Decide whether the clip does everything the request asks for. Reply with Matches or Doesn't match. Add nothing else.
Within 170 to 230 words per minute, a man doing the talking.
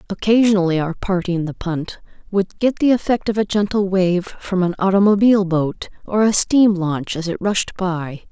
Doesn't match